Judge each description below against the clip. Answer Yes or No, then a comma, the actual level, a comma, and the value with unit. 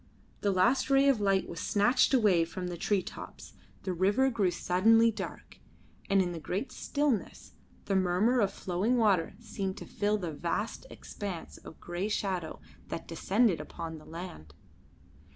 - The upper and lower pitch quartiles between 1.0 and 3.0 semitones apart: No, average, 4.0 semitones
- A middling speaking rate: Yes, average, 165 wpm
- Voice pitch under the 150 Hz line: No, high, 195 Hz